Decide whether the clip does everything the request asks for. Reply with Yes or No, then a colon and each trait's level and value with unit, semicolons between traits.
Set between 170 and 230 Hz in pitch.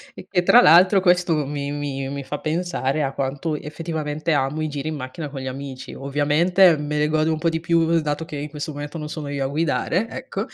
No: medium, 150 Hz